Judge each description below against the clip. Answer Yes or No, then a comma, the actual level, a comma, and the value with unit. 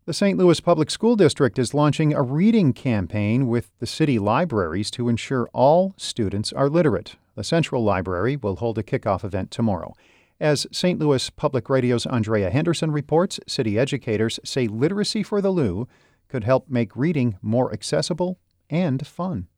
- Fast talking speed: No, average, 160 wpm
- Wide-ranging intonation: Yes, wide, 6.1 semitones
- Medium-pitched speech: No, low, 130 Hz